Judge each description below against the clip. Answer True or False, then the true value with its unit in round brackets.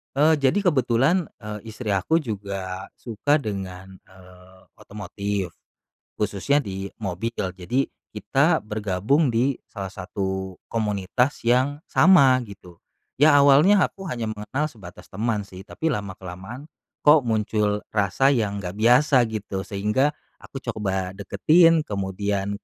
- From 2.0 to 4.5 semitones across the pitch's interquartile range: False (5.6 semitones)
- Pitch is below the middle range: True (105 Hz)